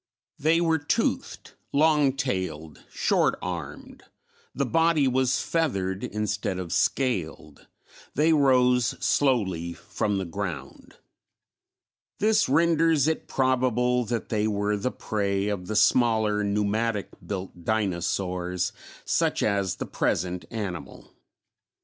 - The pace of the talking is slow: Yes, slow, 110 wpm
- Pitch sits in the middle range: No, low, 110 Hz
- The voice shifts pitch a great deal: Yes, wide, 5.8 semitones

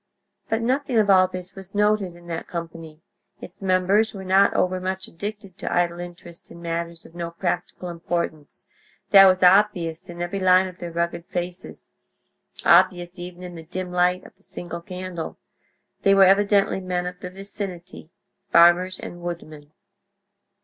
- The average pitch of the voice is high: No, medium, 180 Hz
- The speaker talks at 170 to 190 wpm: No, average, 155 wpm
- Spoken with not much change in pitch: Yes, narrow, 1.9 semitones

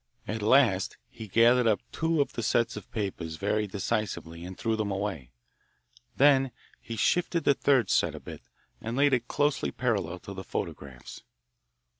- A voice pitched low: Yes, low, 110 Hz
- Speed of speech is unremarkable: Yes, average, 165 wpm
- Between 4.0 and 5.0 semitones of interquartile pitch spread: Yes, average, 4.6 semitones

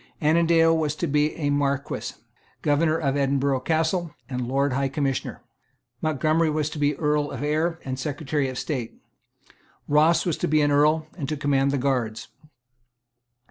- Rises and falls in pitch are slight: Yes, narrow, 2.2 semitones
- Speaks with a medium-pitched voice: Yes, medium, 145 Hz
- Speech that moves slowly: No, average, 160 wpm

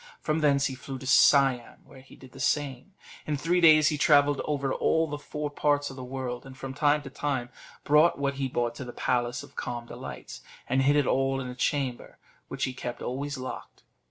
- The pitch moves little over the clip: Yes, narrow, 2.2 semitones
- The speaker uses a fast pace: Yes, fast, 215 wpm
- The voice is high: No, low, 135 Hz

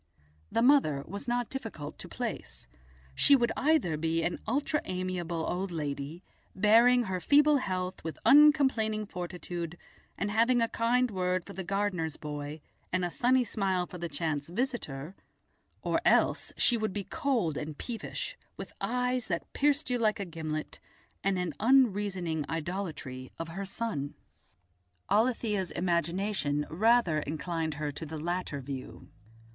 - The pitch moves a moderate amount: No, wide, 6.2 semitones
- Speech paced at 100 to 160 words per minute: Yes, average, 145 wpm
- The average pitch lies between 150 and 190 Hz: Yes, medium, 185 Hz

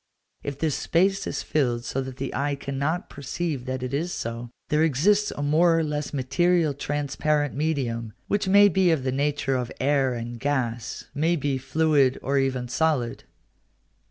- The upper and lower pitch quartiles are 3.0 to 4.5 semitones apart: Yes, average, 3.5 semitones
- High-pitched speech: No, medium, 145 Hz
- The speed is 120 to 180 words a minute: Yes, average, 170 wpm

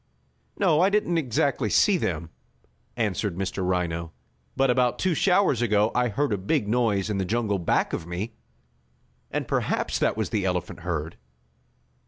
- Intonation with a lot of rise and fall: Yes, wide, 6.6 semitones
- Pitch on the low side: Yes, low, 110 Hz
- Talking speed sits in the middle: Yes, average, 160 wpm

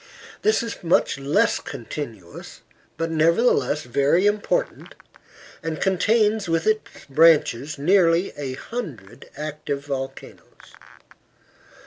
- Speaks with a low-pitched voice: No, medium, 160 Hz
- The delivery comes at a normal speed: No, slow, 95 wpm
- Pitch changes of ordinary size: No, wide, 6.0 semitones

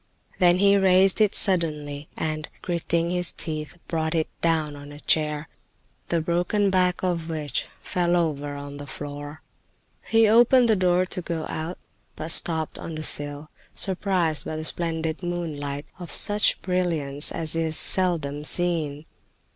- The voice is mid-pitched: Yes, medium, 165 Hz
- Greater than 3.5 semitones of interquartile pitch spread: No, average, 3.0 semitones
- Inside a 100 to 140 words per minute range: No, average, 150 wpm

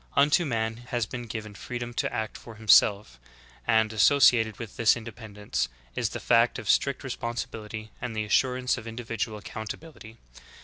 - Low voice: Yes, low, 110 Hz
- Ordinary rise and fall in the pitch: No, narrow, 2.0 semitones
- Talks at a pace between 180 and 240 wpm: No, average, 165 wpm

